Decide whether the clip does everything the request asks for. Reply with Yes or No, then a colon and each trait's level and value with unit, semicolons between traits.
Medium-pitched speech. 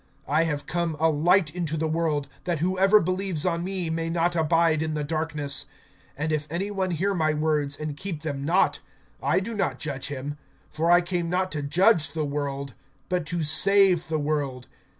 Yes: medium, 160 Hz